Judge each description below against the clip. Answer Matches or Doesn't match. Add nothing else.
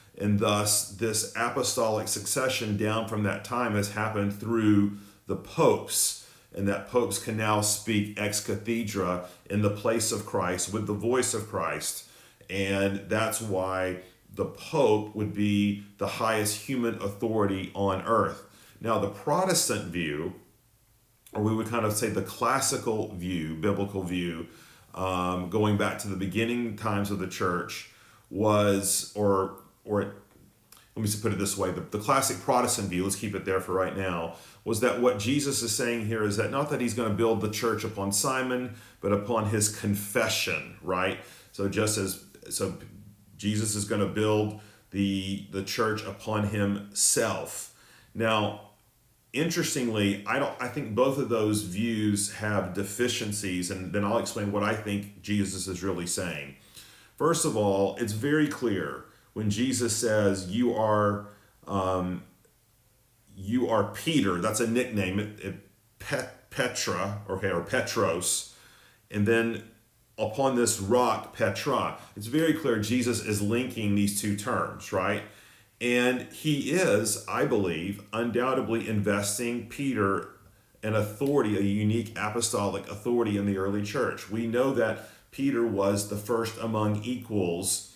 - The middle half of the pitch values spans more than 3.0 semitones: Doesn't match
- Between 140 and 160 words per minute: Matches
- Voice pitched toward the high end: Doesn't match